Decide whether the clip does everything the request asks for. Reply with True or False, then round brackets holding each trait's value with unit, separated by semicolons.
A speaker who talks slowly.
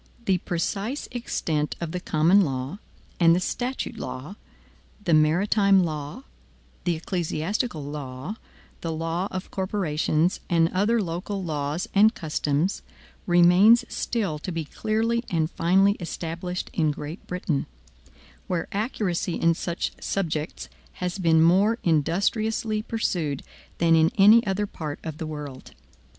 True (130 wpm)